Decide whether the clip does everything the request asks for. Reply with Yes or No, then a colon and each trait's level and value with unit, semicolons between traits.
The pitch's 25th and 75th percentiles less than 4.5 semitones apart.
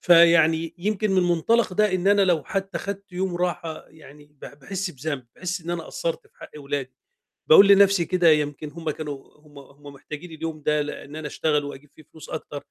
Yes: average, 3.7 semitones